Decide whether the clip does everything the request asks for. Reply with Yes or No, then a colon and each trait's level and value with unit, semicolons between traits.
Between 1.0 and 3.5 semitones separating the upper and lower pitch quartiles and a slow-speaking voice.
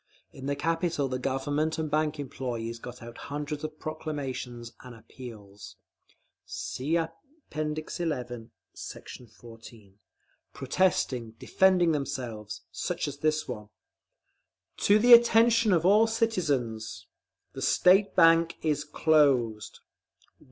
No: average, 5.3 semitones; slow, 110 wpm